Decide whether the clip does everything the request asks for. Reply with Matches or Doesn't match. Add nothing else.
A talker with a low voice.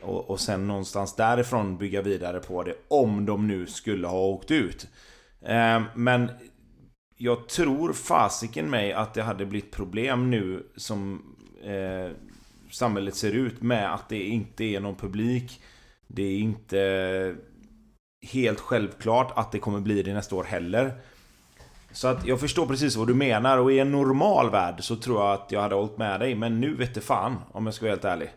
Matches